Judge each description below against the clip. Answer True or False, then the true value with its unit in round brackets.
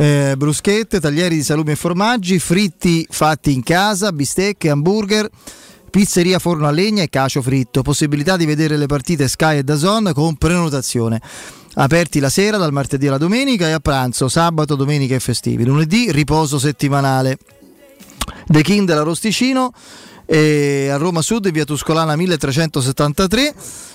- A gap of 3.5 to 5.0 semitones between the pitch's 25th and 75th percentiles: True (4.6 semitones)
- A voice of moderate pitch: True (155 Hz)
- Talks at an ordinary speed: True (145 wpm)